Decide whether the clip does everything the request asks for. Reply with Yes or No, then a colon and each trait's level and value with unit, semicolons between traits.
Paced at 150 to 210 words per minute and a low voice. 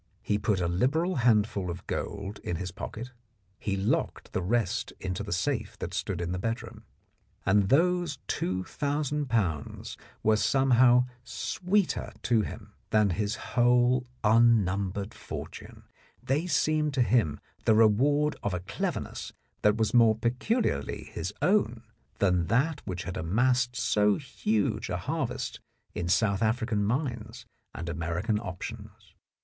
No: average, 140 wpm; low, 110 Hz